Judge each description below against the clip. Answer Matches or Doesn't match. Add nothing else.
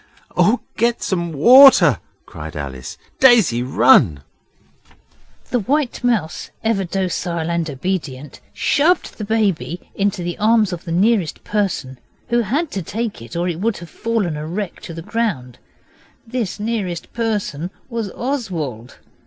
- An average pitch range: Doesn't match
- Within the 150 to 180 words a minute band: Doesn't match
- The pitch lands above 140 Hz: Matches